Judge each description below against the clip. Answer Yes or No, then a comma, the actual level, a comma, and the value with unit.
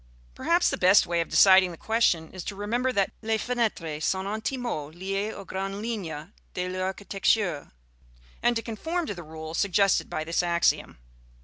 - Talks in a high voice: Yes, high, 195 Hz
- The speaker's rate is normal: Yes, average, 170 wpm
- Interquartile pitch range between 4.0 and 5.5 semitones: Yes, average, 4.3 semitones